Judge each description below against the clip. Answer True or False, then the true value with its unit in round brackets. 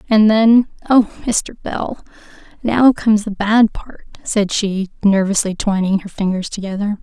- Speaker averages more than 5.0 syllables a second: False (4.2 syllables/s)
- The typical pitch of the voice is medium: False (210 Hz)